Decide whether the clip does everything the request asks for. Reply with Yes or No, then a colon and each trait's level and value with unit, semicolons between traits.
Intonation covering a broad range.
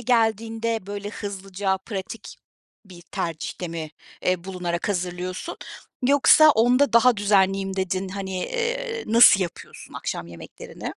No: average, 3.8 semitones